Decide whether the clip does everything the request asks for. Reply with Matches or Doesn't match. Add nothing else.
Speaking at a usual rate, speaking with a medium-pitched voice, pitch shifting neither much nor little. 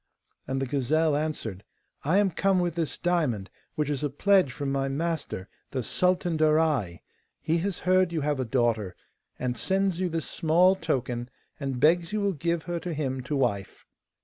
Matches